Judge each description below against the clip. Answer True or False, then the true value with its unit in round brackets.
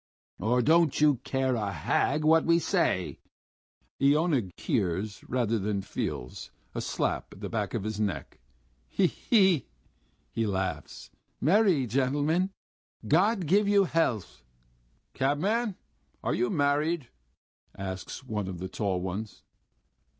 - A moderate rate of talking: False (130 wpm)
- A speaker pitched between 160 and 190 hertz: False (130 Hz)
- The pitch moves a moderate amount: False (8.1 semitones)